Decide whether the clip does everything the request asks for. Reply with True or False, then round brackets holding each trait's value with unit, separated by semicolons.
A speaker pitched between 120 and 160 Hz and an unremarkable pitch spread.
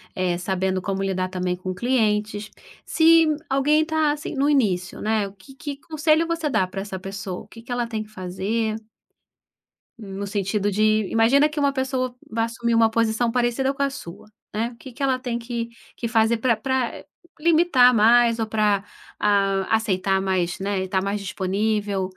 False (220 Hz; 4.8 semitones)